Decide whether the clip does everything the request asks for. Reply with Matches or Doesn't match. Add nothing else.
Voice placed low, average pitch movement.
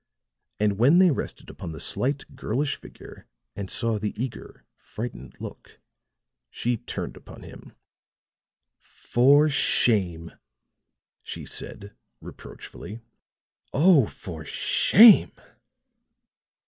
Doesn't match